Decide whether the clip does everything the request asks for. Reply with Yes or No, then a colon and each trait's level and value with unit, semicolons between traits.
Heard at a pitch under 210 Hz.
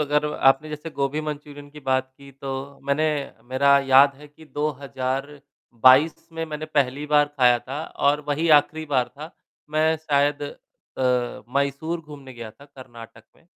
Yes: medium, 140 Hz